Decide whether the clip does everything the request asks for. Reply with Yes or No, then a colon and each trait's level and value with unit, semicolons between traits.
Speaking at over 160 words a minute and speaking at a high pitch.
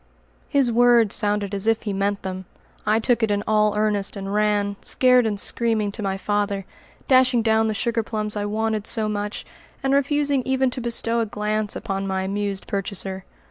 Yes: average, 185 wpm; high, 210 Hz